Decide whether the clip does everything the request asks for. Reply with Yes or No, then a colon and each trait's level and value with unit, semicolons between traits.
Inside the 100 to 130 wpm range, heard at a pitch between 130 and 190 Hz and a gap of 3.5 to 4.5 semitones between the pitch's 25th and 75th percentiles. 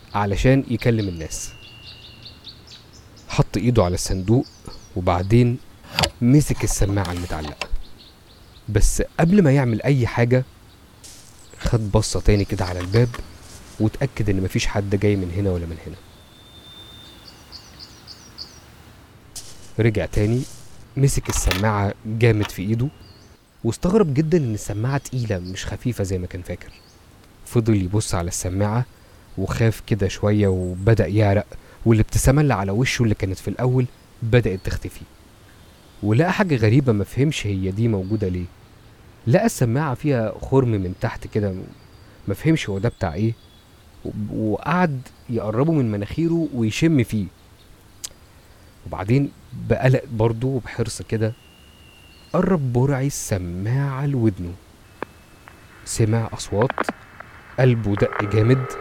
No: average, 110 wpm; low, 110 Hz; average, 3.8 semitones